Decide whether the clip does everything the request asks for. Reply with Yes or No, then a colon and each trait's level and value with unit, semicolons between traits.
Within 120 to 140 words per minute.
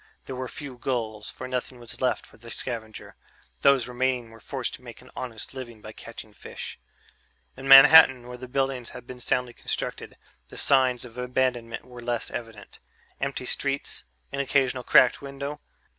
No: average, 175 wpm